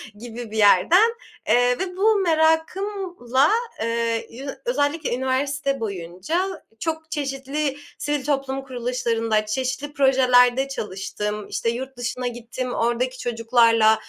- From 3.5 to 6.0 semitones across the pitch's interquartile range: Yes, average, 4.1 semitones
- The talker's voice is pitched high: Yes, very high, 255 Hz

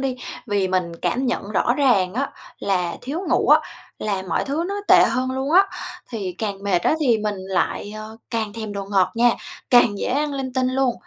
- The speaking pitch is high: Yes, high, 225 Hz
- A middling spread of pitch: Yes, average, 4.9 semitones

